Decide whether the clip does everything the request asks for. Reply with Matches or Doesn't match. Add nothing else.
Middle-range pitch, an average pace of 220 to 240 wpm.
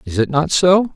Doesn't match